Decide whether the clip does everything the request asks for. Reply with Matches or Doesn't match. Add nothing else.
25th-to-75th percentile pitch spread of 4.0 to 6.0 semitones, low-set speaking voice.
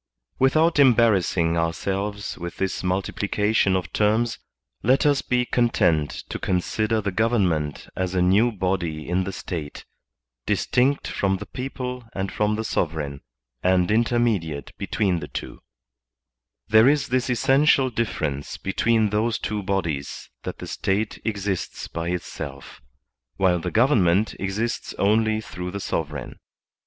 Matches